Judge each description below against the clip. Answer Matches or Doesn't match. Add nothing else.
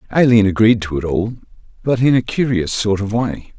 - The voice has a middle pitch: Doesn't match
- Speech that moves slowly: Doesn't match